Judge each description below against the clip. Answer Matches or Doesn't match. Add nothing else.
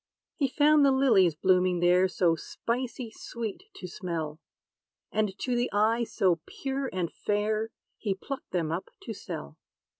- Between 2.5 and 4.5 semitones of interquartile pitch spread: Doesn't match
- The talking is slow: Doesn't match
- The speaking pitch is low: Doesn't match